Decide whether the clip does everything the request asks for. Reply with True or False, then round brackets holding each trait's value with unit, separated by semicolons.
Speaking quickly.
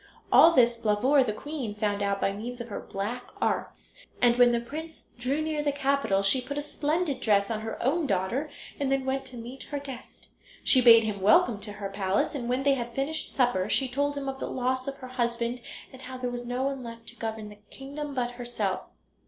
True (225 wpm)